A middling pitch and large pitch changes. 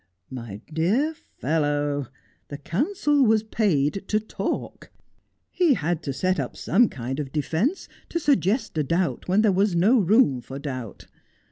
Yes: medium, 175 Hz; wide, 7.5 semitones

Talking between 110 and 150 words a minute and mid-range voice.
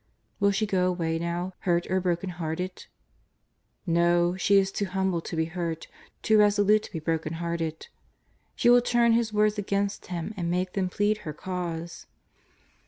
No: average, 160 wpm; medium, 180 Hz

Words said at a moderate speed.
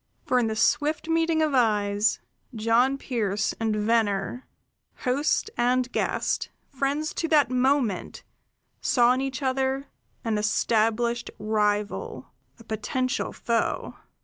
No: slow, 120 wpm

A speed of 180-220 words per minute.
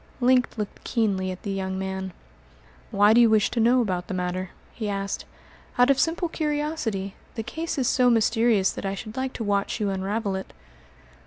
Yes: average, 190 wpm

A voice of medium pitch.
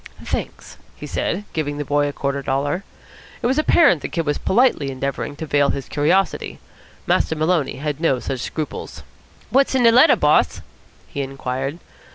Yes: medium, 145 Hz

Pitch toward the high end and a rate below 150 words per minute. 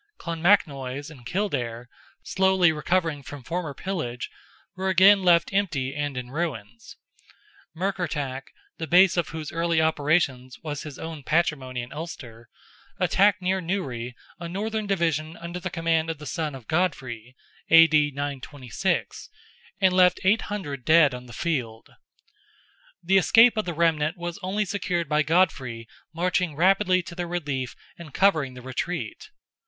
No: medium, 160 Hz; average, 140 wpm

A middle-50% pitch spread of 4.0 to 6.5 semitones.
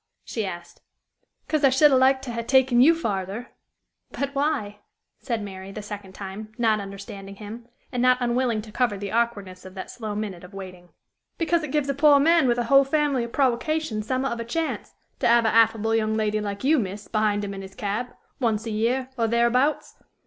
Yes: average, 4.3 semitones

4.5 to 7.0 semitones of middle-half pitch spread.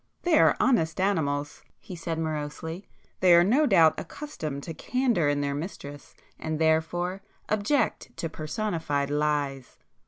Yes: average, 4.9 semitones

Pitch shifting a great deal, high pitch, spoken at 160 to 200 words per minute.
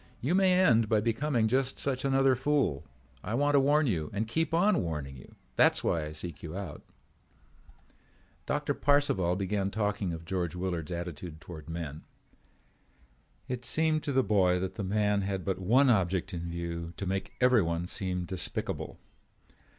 No: wide, 7.1 semitones; low, 100 Hz; average, 165 wpm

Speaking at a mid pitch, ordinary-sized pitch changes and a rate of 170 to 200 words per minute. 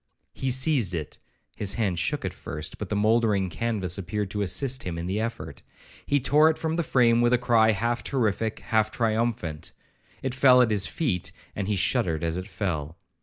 No: low, 110 Hz; average, 4.5 semitones; average, 185 wpm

